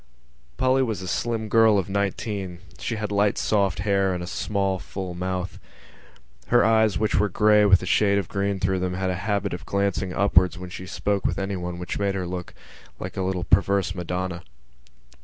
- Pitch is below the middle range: Yes, very low, 95 Hz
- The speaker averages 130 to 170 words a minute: No, average, 195 wpm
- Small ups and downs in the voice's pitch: Yes, narrow, 1.9 semitones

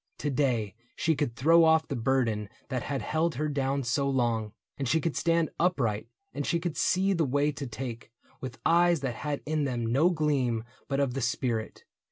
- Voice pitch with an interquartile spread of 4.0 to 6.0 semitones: Yes, average, 4.5 semitones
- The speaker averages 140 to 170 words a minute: No, average, 200 wpm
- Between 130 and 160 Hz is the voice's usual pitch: Yes, medium, 140 Hz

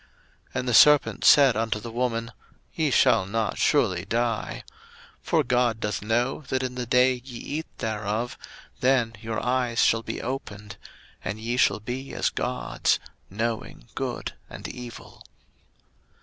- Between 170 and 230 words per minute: No, average, 150 wpm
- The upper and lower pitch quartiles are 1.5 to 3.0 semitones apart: Yes, narrow, 2.4 semitones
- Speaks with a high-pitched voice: No, low, 120 Hz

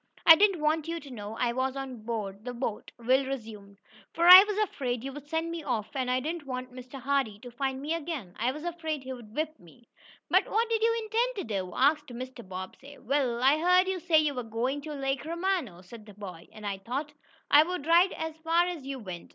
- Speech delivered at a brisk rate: Yes, fast, 225 wpm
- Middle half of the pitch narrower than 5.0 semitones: No, wide, 5.5 semitones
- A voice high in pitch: Yes, very high, 270 Hz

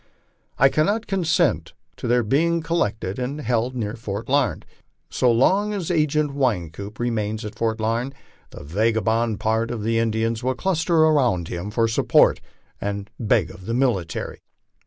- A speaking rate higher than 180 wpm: No, average, 155 wpm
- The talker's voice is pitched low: Yes, low, 115 Hz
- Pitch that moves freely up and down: No, average, 4.7 semitones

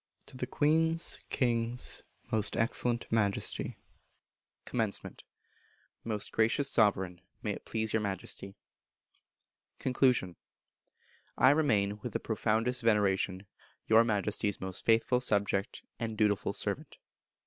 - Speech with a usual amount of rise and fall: Yes, average, 3.2 semitones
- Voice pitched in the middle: No, low, 110 Hz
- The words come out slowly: Yes, slow, 105 wpm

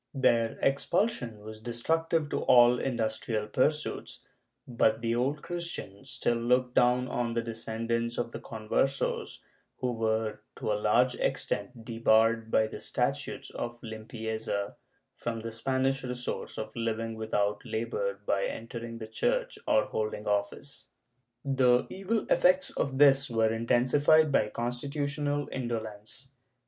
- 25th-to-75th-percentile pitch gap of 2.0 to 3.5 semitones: Yes, average, 3.2 semitones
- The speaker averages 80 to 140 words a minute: Yes, slow, 135 wpm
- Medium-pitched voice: No, low, 120 Hz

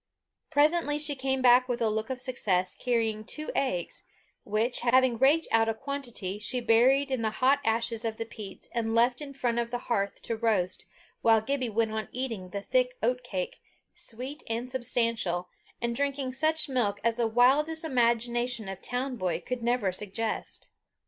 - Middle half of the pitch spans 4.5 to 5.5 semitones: No, average, 2.9 semitones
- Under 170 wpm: No, average, 175 wpm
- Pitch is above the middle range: Yes, high, 240 Hz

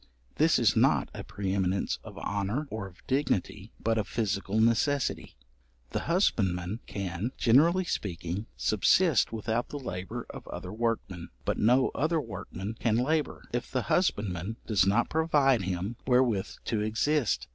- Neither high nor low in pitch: No, low, 110 Hz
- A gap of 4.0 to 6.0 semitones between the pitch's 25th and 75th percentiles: Yes, average, 5.1 semitones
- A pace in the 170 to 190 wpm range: No, average, 145 wpm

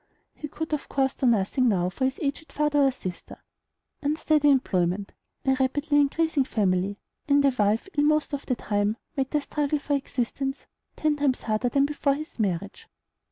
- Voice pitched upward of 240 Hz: Yes, very high, 270 Hz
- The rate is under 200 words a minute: Yes, average, 175 wpm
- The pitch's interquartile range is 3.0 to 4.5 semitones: No, average, 5.2 semitones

